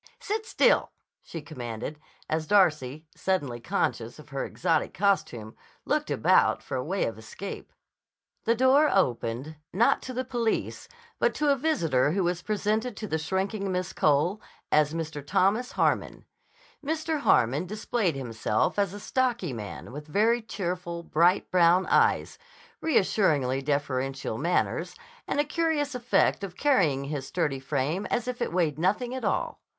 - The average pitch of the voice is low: No, medium, 175 Hz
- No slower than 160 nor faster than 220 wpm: No, average, 150 wpm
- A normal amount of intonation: No, wide, 7.6 semitones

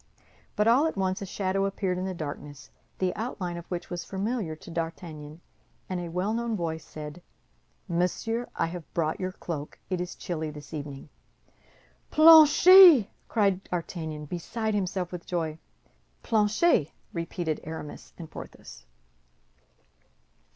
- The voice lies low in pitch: No, medium, 180 Hz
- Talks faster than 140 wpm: No, slow, 135 wpm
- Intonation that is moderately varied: Yes, average, 4.2 semitones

